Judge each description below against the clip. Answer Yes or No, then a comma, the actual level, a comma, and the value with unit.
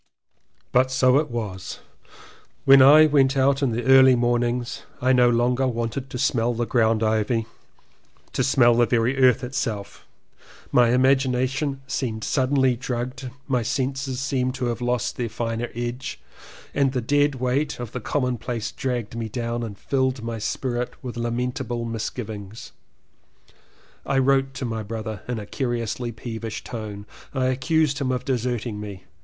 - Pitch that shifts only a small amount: Yes, narrow, 2.2 semitones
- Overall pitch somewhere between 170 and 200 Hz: No, low, 125 Hz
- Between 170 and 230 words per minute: No, average, 150 wpm